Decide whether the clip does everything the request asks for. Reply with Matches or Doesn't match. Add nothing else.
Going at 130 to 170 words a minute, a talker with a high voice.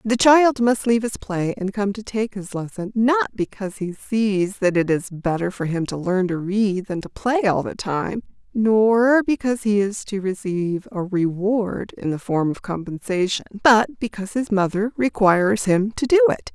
Doesn't match